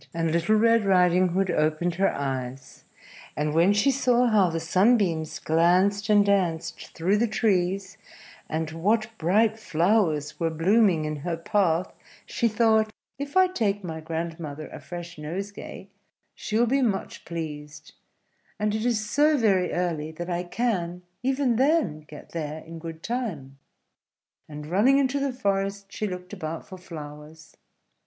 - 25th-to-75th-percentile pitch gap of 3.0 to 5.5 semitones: Yes, average, 5.1 semitones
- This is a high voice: No, medium, 180 Hz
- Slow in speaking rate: No, average, 150 wpm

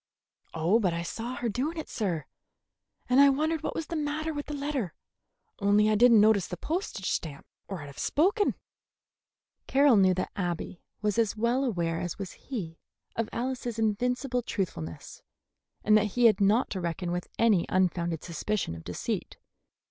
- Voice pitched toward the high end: Yes, high, 215 Hz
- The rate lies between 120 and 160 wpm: No, average, 175 wpm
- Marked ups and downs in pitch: Yes, wide, 6.2 semitones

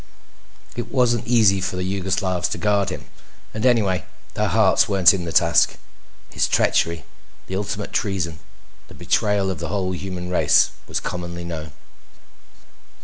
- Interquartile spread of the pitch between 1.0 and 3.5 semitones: Yes, narrow, 2.5 semitones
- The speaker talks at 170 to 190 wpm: No, average, 145 wpm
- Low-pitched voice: Yes, very low, 95 Hz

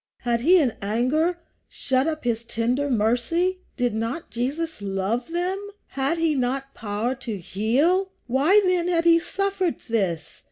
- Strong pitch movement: Yes, wide, 6.5 semitones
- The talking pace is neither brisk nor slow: Yes, average, 150 wpm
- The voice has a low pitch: No, very high, 265 Hz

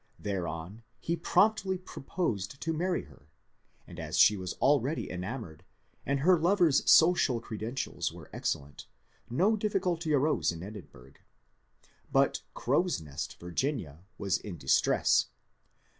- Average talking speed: No, slow, 130 wpm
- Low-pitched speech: Yes, low, 130 Hz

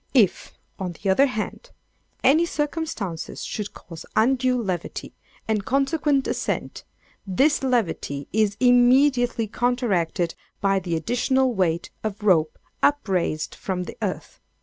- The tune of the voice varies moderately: No, wide, 6.0 semitones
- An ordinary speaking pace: No, slow, 120 wpm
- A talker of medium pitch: No, high, 220 Hz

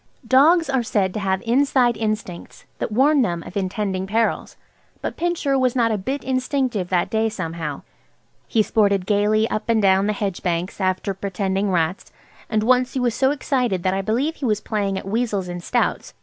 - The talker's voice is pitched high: Yes, high, 215 Hz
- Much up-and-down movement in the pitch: No, average, 4.7 semitones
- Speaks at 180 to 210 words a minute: Yes, average, 190 wpm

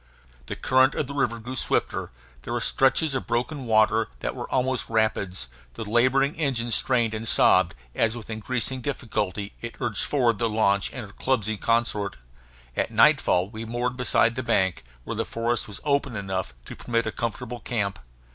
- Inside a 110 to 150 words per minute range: No, average, 175 wpm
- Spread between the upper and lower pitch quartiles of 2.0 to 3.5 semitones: Yes, average, 2.9 semitones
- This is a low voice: Yes, low, 115 Hz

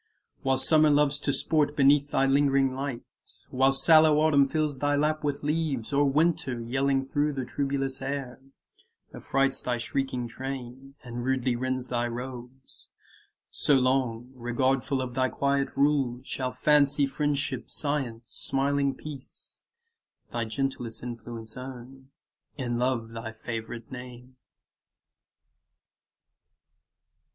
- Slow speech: Yes, slow, 125 wpm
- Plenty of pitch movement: No, narrow, 2.4 semitones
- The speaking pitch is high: No, low, 135 Hz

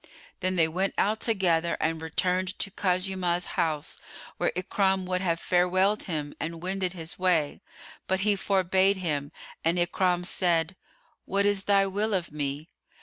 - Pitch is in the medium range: Yes, medium, 180 Hz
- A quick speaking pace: No, average, 150 wpm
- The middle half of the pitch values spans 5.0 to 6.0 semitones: No, narrow, 2.5 semitones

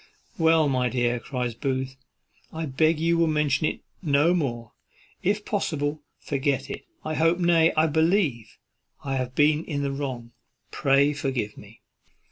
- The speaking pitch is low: No, medium, 145 Hz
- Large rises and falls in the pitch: No, average, 3.7 semitones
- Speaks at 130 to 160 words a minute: Yes, average, 150 wpm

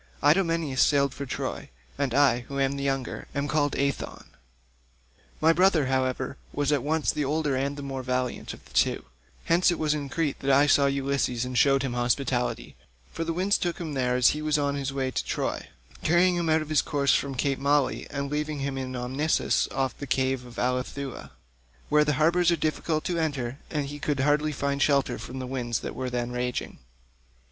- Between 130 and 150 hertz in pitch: Yes, medium, 140 Hz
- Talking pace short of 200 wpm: No, fast, 205 wpm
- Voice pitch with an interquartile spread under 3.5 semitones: Yes, narrow, 2.4 semitones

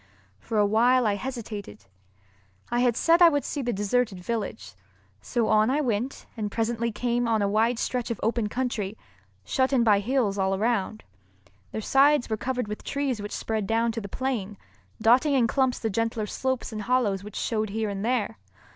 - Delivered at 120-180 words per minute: No, average, 190 wpm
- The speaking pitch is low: No, high, 230 Hz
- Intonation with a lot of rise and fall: No, average, 3.1 semitones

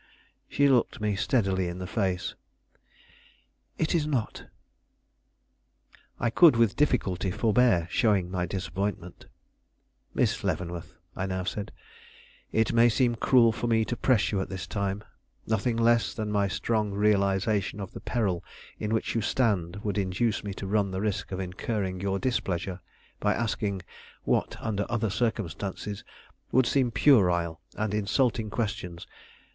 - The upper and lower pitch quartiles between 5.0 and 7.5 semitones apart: No, average, 3.4 semitones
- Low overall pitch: Yes, low, 105 Hz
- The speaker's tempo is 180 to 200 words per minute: No, average, 145 wpm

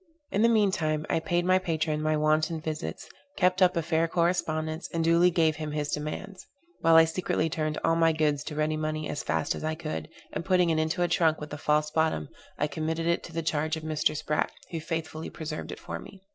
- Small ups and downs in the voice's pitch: Yes, narrow, 1.5 semitones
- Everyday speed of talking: No, fast, 230 wpm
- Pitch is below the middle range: No, medium, 160 Hz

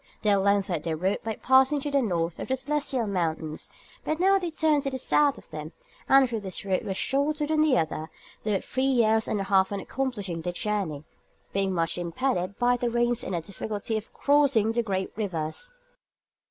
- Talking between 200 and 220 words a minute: Yes, fast, 205 wpm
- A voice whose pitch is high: Yes, high, 215 Hz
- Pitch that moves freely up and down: Yes, wide, 6.2 semitones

